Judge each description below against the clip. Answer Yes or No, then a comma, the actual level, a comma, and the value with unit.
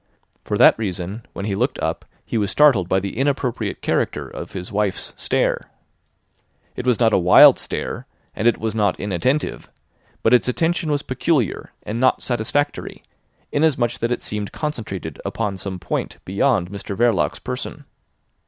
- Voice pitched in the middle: No, low, 115 Hz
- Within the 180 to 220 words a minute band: No, average, 160 wpm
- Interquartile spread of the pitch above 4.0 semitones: Yes, average, 4.8 semitones